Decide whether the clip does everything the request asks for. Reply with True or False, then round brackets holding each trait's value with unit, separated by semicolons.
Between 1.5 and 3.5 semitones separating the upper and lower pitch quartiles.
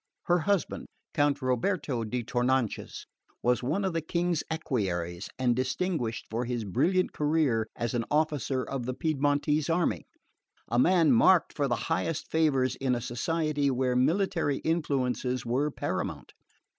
False (4.7 semitones)